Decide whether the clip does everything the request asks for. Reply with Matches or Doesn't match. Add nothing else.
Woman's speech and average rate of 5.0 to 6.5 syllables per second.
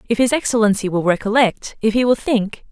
Matches